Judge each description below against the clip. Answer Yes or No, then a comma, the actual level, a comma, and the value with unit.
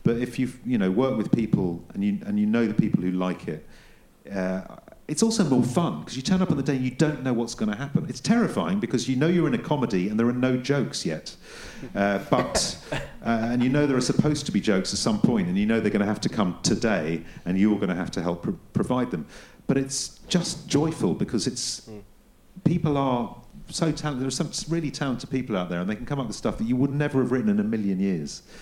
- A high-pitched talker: No, low, 130 Hz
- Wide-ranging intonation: Yes, wide, 7.0 semitones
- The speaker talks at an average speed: No, fast, 260 wpm